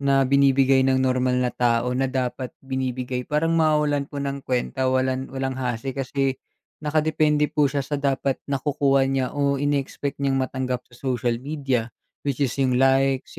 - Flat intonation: Yes, narrow, 1.5 semitones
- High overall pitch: No, low, 135 Hz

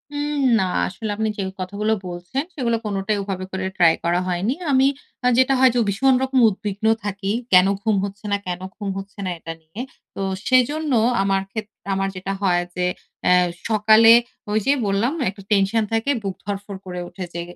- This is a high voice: Yes, high, 200 Hz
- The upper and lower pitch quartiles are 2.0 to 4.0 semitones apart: Yes, average, 3.1 semitones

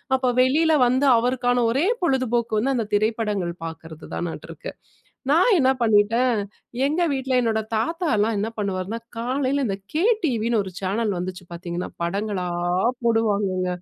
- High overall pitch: Yes, high, 225 Hz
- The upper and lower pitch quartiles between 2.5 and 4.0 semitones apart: No, average, 4.5 semitones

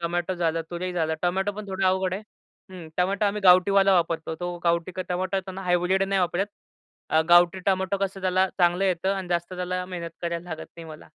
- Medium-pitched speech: Yes, medium, 180 Hz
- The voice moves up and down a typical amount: No, narrow, 1.7 semitones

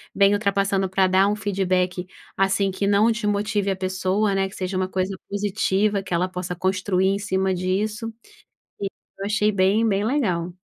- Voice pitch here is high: Yes, high, 195 Hz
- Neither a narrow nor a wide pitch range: No, narrow, 1.6 semitones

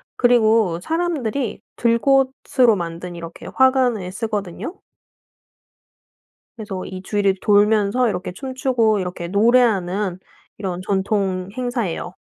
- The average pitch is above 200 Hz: Yes, high, 210 Hz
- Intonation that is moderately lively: Yes, average, 4.9 semitones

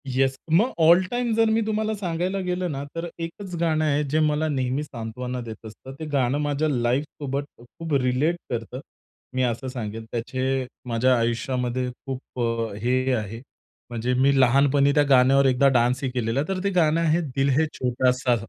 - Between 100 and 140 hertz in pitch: Yes, low, 135 Hz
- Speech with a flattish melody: No, average, 4.0 semitones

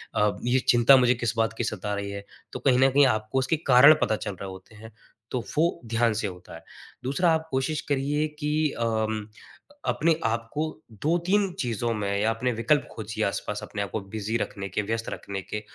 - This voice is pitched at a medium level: No, low, 115 Hz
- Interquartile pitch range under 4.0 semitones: No, average, 4.5 semitones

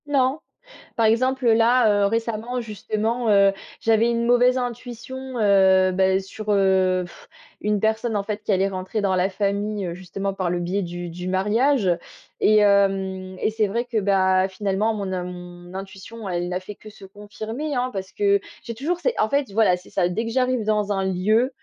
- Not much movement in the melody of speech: No, average, 3.3 semitones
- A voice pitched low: No, high, 205 Hz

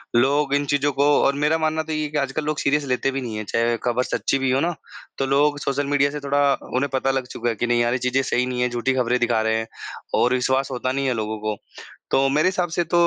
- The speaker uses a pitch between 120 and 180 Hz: Yes, low, 135 Hz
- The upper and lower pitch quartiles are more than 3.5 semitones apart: No, average, 2.7 semitones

